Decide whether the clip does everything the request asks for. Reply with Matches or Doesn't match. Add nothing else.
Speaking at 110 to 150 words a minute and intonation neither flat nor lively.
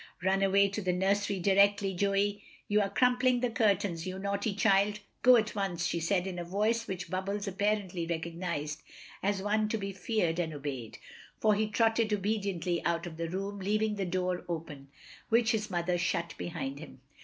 Doesn't match